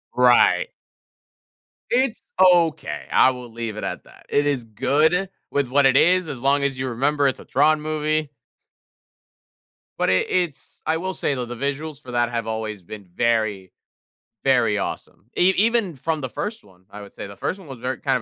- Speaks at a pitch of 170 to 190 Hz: No, medium, 140 Hz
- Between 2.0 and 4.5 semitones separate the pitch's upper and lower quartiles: No, average, 5.0 semitones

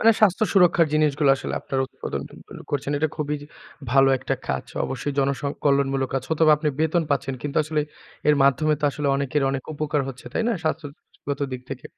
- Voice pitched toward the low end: No, medium, 145 Hz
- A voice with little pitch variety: Yes, narrow, 2.2 semitones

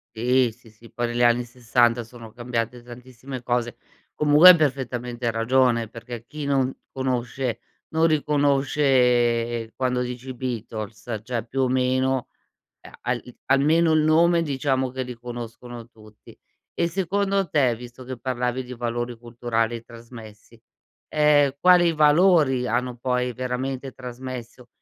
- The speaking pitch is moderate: No, low, 125 Hz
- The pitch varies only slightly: Yes, narrow, 2.2 semitones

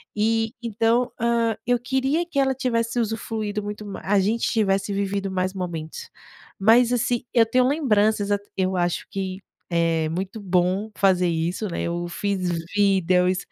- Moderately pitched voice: No, high, 205 Hz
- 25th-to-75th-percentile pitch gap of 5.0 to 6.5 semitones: No, average, 3.7 semitones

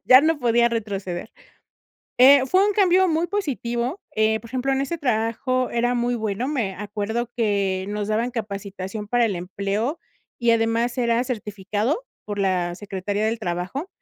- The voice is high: Yes, high, 230 Hz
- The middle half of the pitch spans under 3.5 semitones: No, average, 3.8 semitones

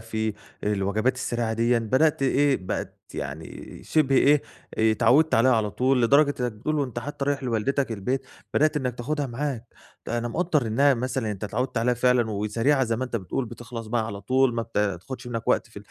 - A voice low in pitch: Yes, low, 120 Hz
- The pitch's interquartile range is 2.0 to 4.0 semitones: Yes, average, 3.3 semitones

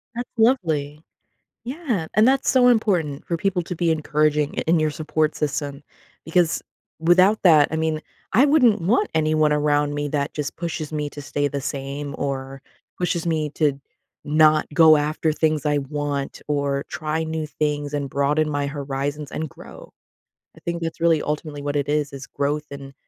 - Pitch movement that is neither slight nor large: No, narrow, 2.3 semitones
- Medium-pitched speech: Yes, medium, 150 Hz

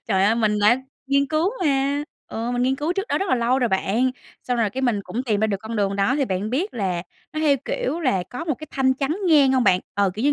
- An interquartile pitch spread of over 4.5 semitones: Yes, average, 5.0 semitones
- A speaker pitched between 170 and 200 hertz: No, very high, 250 Hz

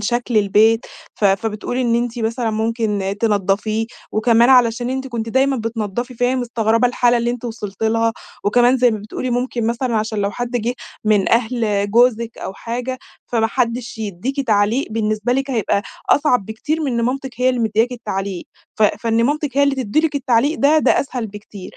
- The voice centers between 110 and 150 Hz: No, high, 230 Hz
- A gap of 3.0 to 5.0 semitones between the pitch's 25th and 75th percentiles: No, narrow, 2.5 semitones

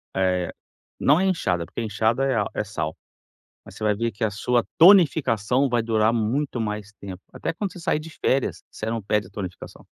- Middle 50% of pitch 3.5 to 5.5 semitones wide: Yes, average, 4.6 semitones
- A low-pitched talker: Yes, low, 115 Hz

